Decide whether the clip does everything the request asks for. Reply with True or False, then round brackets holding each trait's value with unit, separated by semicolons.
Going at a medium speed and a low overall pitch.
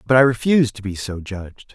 False (240 wpm; 115 Hz)